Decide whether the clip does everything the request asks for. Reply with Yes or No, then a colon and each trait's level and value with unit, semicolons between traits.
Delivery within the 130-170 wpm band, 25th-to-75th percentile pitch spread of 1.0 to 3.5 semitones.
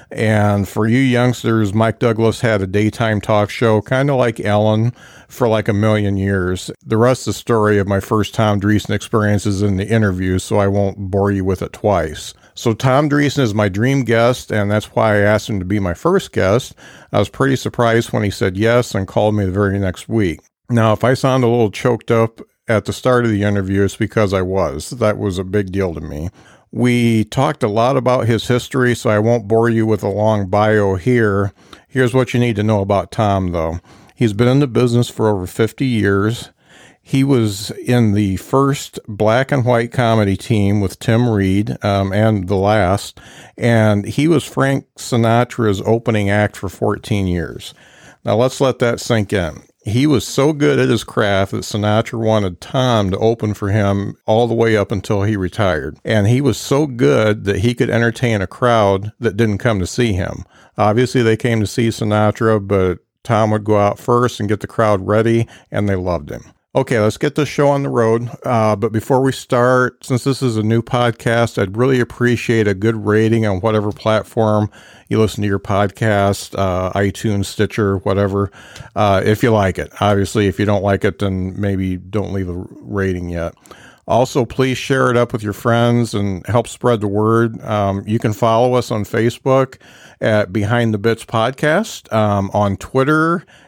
No: average, 200 wpm; average, 3.0 semitones